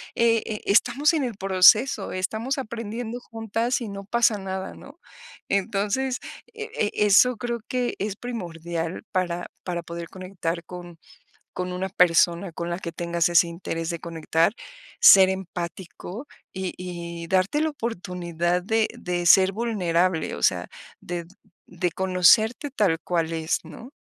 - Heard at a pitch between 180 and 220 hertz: Yes, high, 190 Hz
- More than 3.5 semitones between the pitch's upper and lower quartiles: Yes, average, 4.7 semitones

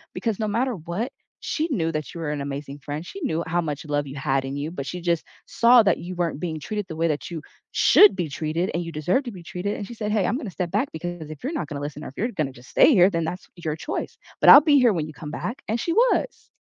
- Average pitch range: No, wide, 5.8 semitones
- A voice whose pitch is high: No, medium, 170 Hz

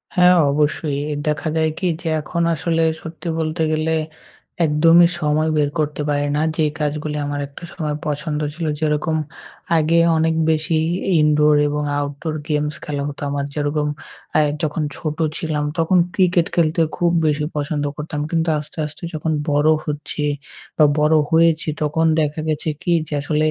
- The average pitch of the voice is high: No, medium, 155 Hz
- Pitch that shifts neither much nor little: No, narrow, 1.5 semitones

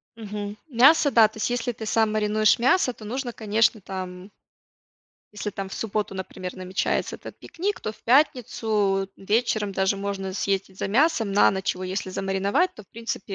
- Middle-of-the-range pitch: No, high, 210 Hz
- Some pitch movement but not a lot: Yes, average, 3.0 semitones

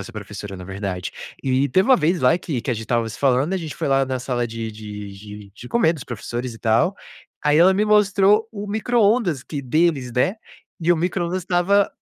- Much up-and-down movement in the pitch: Yes, wide, 8.6 semitones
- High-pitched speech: No, low, 135 Hz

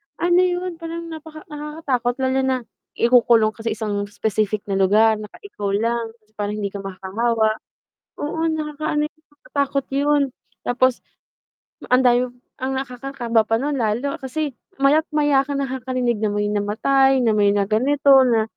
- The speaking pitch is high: Yes, very high, 255 Hz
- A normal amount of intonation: Yes, average, 5.0 semitones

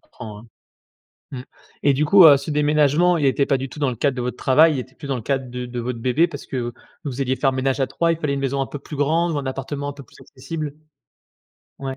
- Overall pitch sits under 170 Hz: Yes, medium, 140 Hz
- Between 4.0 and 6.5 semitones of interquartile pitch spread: No, narrow, 2.4 semitones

